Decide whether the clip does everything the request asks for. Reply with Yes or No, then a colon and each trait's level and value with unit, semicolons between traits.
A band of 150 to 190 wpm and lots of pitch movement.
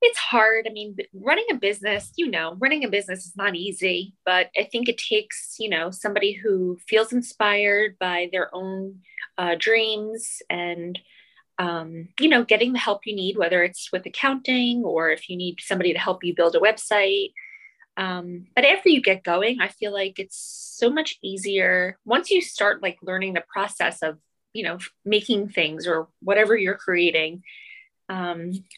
No: average, 175 wpm; average, 4.2 semitones